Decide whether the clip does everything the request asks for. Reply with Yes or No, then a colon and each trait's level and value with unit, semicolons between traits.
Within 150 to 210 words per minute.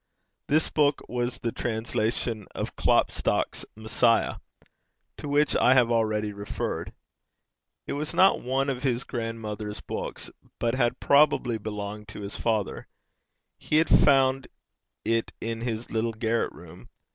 No: slow, 135 wpm